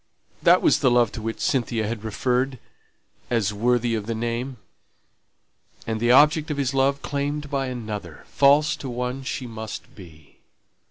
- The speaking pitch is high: No, low, 125 Hz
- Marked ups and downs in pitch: No, average, 3.5 semitones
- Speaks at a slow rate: No, average, 160 wpm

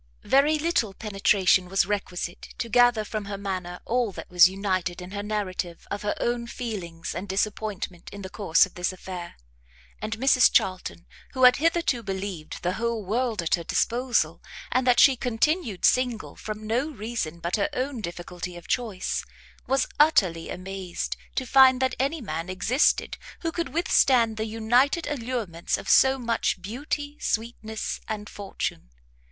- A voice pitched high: Yes, high, 215 Hz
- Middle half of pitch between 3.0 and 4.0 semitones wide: No, average, 5.1 semitones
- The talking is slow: No, average, 160 wpm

